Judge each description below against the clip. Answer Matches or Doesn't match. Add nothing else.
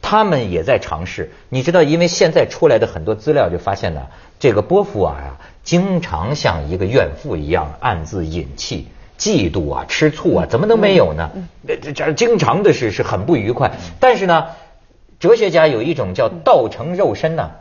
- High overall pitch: Doesn't match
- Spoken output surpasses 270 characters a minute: Matches